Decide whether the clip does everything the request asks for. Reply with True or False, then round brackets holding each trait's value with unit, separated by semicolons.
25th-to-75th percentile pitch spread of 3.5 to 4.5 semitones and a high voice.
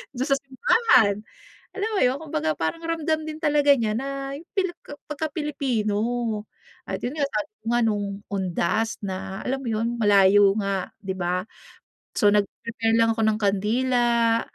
False (5.6 semitones; 230 Hz)